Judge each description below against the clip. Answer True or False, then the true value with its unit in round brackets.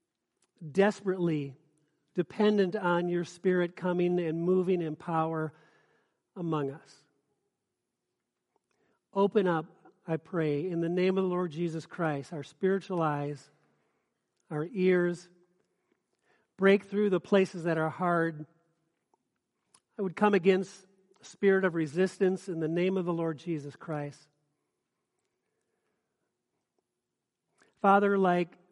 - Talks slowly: True (115 wpm)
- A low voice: False (175 Hz)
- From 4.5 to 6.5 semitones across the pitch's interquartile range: False (3.1 semitones)